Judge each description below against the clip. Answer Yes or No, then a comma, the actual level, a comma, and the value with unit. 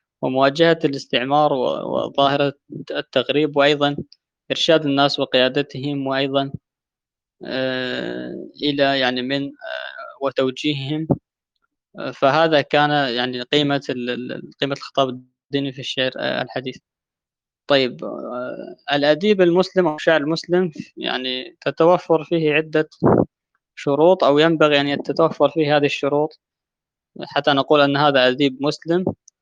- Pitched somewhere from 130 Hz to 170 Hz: Yes, medium, 140 Hz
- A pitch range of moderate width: No, narrow, 2.2 semitones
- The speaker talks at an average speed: Yes, average, 100 wpm